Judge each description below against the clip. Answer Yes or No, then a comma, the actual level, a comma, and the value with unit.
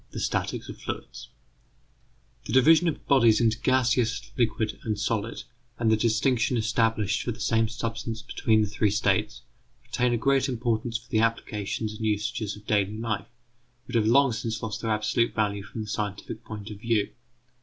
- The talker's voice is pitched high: No, low, 110 Hz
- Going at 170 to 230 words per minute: Yes, average, 175 wpm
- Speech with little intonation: Yes, narrow, 1.7 semitones